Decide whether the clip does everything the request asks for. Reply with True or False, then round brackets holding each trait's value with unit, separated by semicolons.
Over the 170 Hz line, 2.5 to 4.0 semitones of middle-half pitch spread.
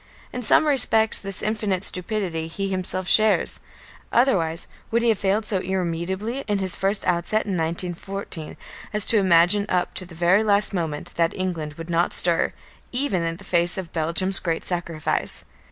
True (185 Hz; 3.5 semitones)